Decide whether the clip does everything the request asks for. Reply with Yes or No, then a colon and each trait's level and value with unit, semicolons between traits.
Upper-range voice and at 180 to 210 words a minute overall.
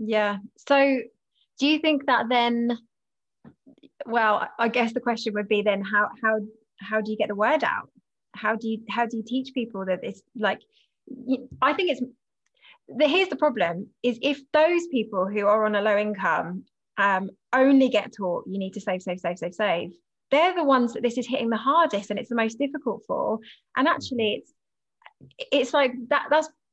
Yes: high, 235 Hz; average, 195 wpm